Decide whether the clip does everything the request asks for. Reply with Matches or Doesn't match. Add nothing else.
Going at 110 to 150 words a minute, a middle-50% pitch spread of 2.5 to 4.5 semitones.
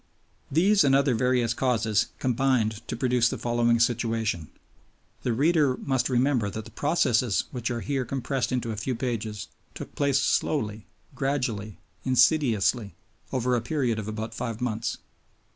Matches